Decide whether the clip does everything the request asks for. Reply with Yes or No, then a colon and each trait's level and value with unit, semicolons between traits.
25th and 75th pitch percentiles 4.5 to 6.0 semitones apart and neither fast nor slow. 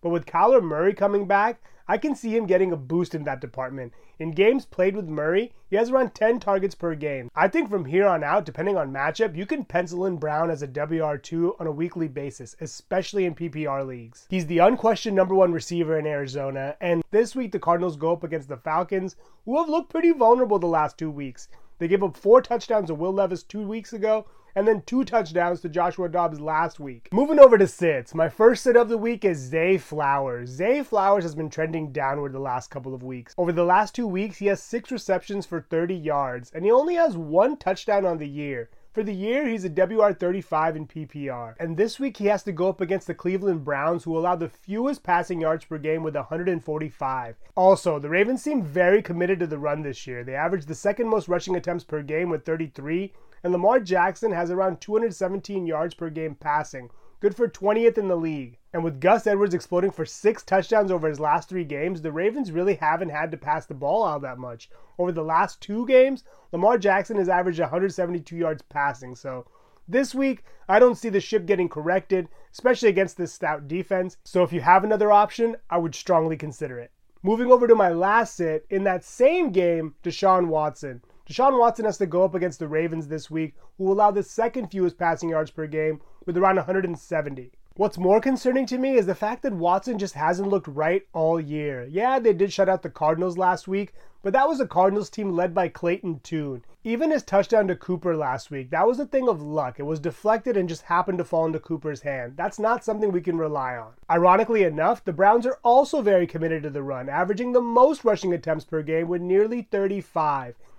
No: average, 4.8 semitones; fast, 215 wpm